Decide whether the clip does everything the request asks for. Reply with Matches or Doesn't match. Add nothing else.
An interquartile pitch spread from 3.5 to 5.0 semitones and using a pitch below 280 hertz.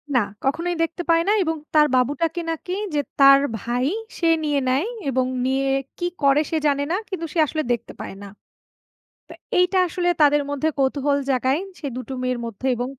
Doesn't match